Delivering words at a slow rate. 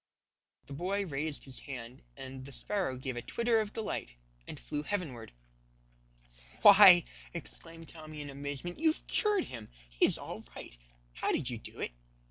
No: average, 160 wpm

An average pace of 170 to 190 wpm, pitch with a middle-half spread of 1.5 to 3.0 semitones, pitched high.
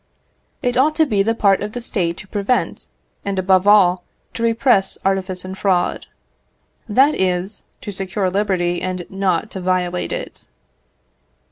No: average, 150 wpm; narrow, 2.4 semitones; high, 195 Hz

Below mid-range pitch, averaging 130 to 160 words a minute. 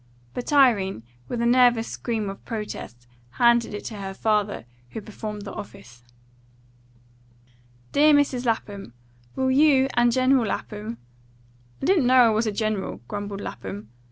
No: high, 220 Hz; average, 150 wpm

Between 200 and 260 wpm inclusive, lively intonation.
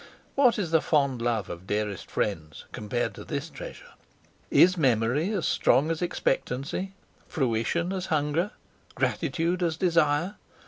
No: slow, 135 wpm; wide, 6.9 semitones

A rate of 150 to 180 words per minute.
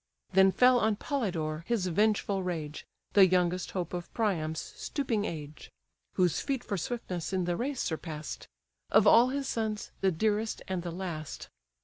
Yes: average, 155 wpm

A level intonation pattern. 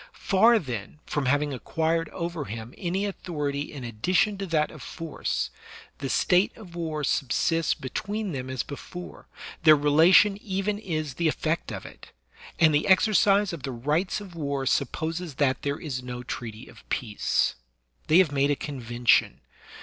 No: average, 4.7 semitones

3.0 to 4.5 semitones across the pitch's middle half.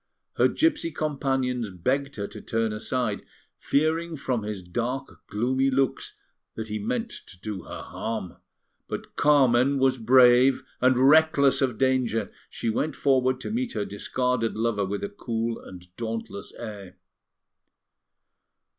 Yes: average, 3.7 semitones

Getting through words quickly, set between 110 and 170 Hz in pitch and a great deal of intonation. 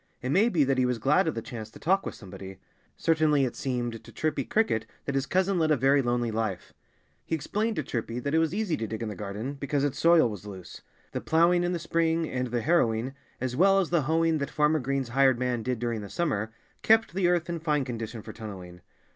Yes: fast, 240 wpm; low, 135 Hz; wide, 6.1 semitones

